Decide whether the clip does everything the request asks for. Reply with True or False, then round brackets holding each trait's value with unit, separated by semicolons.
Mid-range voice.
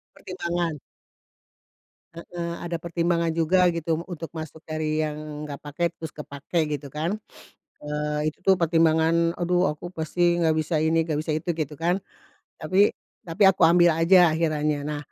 True (165 Hz)